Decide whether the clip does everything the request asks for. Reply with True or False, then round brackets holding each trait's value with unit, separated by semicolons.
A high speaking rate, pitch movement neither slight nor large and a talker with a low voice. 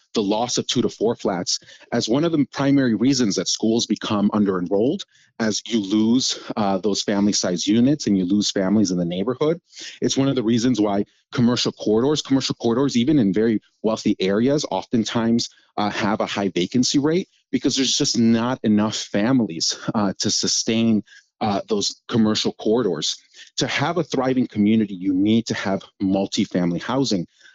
False (170 wpm; 3.9 semitones; 110 Hz)